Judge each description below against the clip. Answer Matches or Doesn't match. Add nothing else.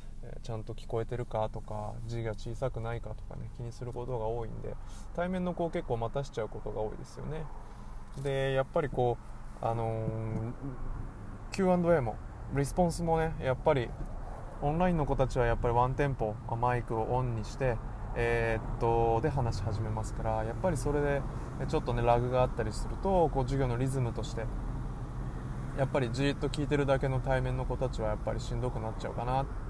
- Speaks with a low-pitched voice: Matches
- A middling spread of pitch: Matches